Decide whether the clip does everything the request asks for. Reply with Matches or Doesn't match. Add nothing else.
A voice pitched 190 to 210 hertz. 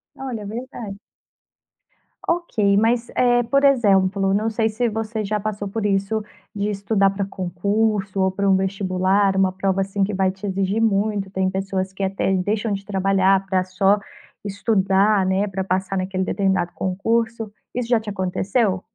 Matches